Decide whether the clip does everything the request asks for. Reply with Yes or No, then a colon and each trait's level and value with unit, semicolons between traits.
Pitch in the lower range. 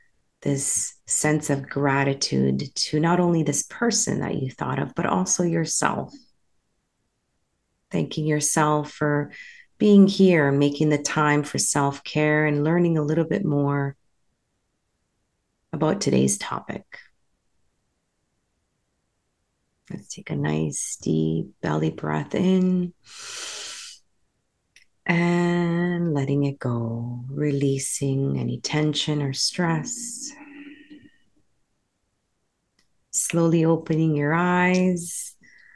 No: medium, 155 Hz